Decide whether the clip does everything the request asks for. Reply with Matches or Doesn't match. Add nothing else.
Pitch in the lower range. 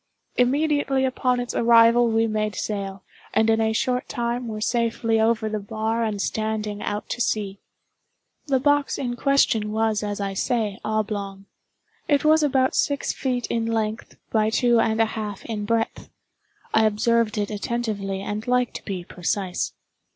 Doesn't match